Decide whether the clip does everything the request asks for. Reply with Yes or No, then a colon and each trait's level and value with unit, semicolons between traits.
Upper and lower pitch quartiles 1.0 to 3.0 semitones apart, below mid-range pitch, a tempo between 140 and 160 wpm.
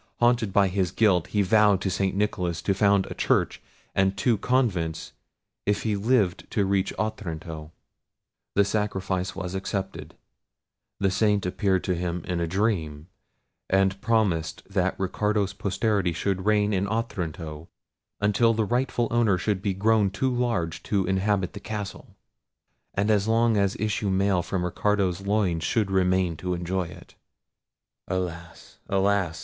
Yes: narrow, 2.6 semitones; very low, 95 Hz; average, 145 wpm